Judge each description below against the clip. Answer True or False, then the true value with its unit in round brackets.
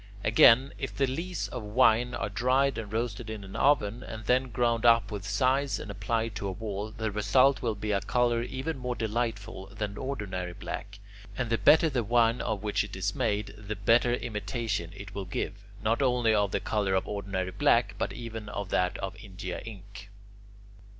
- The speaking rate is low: False (190 wpm)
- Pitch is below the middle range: True (110 Hz)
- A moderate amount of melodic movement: True (3.2 semitones)